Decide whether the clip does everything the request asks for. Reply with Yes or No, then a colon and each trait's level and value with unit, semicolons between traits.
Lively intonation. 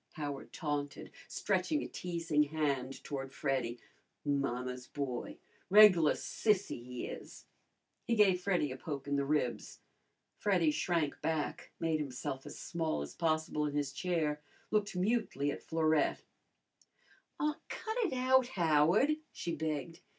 No: average, 4.4 semitones